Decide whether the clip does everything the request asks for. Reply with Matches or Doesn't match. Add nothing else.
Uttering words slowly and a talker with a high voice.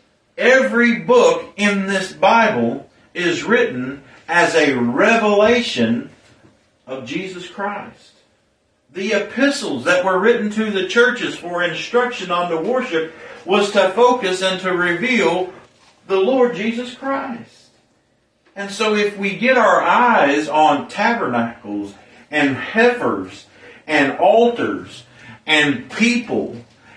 Matches